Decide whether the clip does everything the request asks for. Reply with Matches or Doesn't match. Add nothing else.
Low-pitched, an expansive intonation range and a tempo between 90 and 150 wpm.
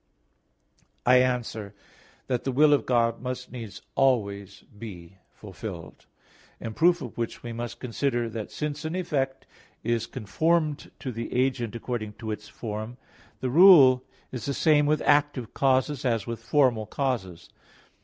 Doesn't match